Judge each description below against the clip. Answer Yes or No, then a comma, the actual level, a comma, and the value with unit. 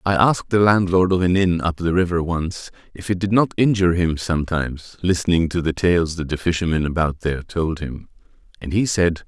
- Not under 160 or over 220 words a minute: Yes, fast, 205 wpm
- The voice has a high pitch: No, very low, 85 Hz